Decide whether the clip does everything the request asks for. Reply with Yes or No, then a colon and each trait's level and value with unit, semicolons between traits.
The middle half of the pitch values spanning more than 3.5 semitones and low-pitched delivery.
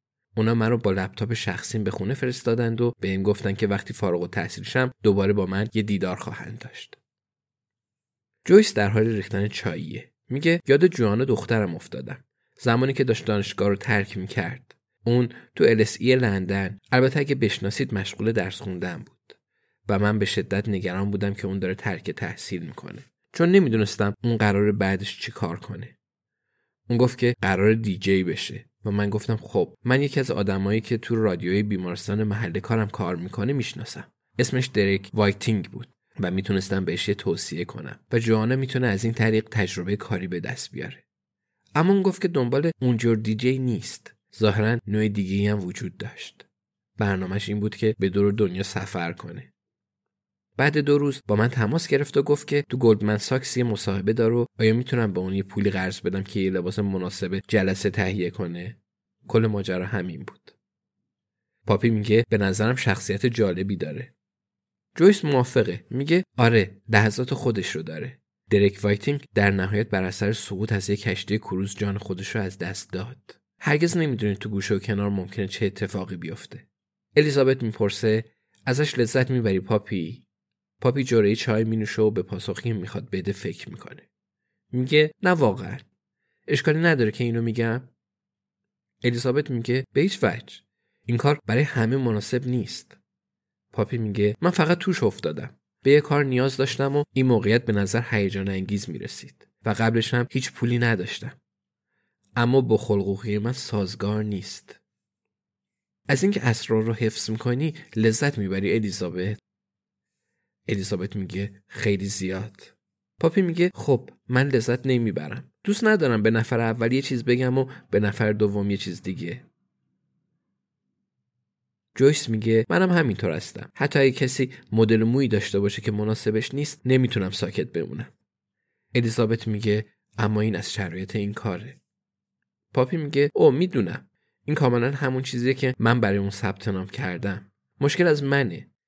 Yes: average, 4.0 semitones; low, 110 Hz